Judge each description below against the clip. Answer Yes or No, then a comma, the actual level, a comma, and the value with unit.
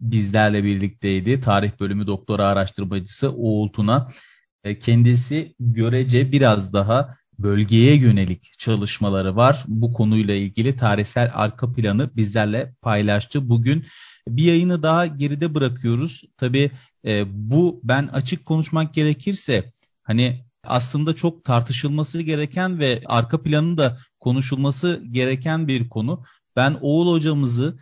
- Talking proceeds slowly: No, average, 110 wpm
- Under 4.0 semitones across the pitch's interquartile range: No, average, 5.1 semitones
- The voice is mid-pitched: No, low, 125 Hz